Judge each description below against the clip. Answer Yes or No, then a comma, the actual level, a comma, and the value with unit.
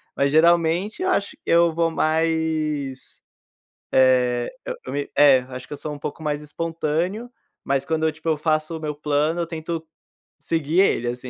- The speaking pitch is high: No, medium, 155 Hz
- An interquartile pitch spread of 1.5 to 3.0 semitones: Yes, narrow, 2.5 semitones